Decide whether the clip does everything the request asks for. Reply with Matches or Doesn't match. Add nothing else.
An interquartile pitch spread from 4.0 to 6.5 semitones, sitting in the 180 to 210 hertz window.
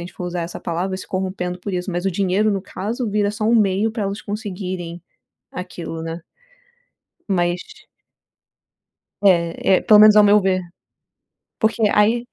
Doesn't match